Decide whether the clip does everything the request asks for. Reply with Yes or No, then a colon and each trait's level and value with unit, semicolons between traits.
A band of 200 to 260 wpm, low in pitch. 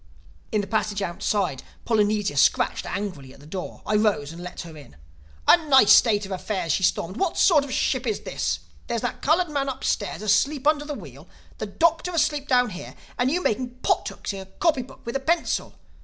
No: fast, 205 wpm; high, 215 Hz